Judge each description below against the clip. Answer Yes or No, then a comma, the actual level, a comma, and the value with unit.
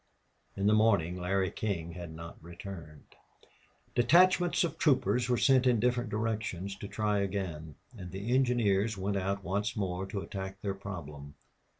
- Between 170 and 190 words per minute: No, average, 155 wpm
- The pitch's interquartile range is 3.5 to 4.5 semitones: Yes, average, 3.8 semitones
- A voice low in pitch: Yes, low, 100 Hz